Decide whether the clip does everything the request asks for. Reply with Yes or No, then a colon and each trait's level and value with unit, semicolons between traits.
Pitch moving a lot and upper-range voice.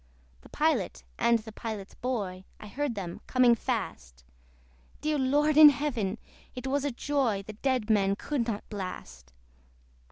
Yes: wide, 5.7 semitones; high, 235 Hz